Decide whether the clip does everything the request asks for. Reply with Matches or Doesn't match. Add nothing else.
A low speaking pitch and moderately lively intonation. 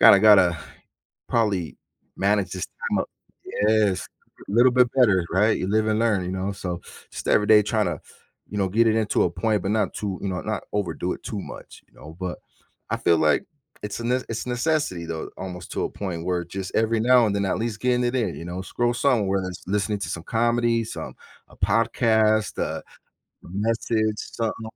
Matches